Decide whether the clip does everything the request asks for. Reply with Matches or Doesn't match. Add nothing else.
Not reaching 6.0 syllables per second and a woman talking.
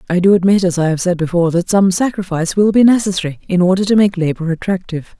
Doesn't match